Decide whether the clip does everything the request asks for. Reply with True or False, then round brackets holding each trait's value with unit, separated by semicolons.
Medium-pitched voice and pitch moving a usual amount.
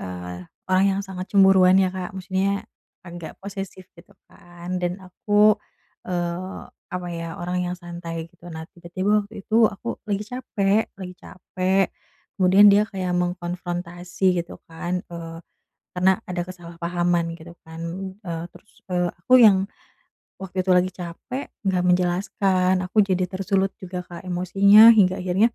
False (180 Hz; 1.7 semitones)